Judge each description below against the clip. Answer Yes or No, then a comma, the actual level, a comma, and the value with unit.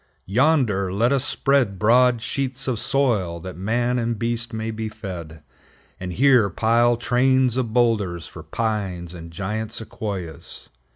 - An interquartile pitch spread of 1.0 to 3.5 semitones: No, average, 4.5 semitones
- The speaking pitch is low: Yes, low, 110 Hz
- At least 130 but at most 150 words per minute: Yes, average, 140 wpm